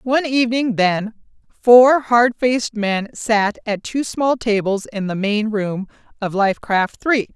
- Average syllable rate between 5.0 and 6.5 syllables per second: No, 4.0 syllables/s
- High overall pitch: Yes, high, 225 Hz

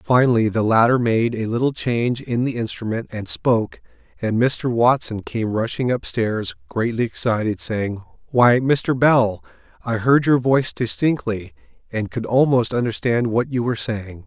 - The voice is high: No, low, 120 Hz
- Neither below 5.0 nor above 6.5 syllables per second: No, 4.6 syllables/s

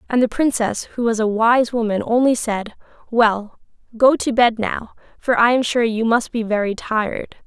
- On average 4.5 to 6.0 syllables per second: Yes, 4.7 syllables/s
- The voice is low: No, high, 230 Hz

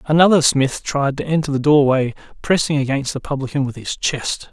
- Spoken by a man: Yes, male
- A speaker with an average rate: Yes, average, 185 wpm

